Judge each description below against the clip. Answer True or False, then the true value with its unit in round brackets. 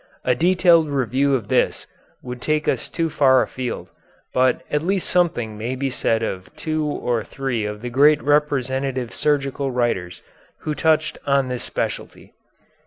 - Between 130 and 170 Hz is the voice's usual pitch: True (135 Hz)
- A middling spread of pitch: True (3.5 semitones)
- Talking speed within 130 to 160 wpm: True (155 wpm)